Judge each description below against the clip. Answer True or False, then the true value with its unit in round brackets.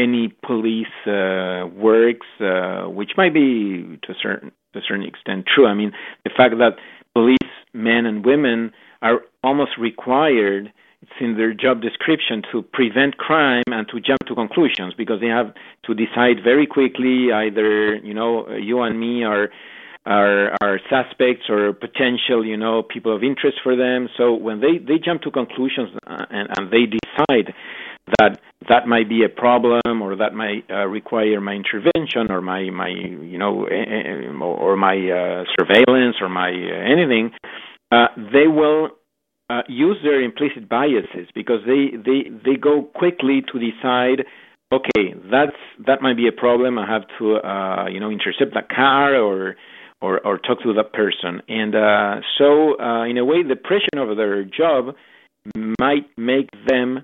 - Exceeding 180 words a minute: False (170 wpm)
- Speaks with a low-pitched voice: True (115 Hz)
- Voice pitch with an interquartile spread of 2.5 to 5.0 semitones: True (3.4 semitones)